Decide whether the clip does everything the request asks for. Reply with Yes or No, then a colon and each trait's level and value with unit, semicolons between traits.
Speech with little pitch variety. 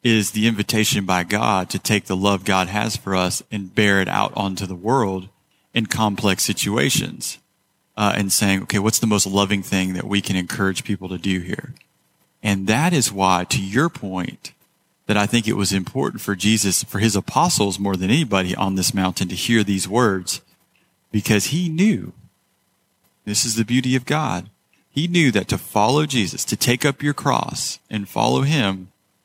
No: average, 3.3 semitones